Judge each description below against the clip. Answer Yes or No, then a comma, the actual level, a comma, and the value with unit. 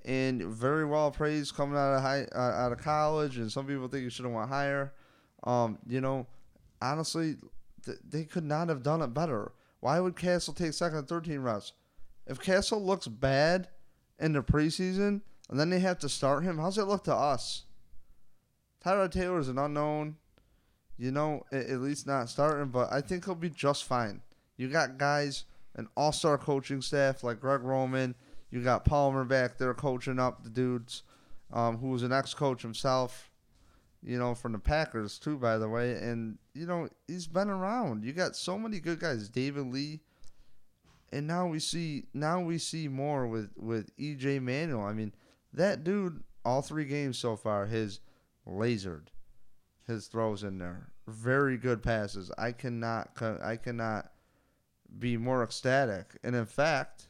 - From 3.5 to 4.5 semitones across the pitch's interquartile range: Yes, average, 4.1 semitones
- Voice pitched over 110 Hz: Yes, low, 135 Hz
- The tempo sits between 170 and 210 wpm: Yes, average, 175 wpm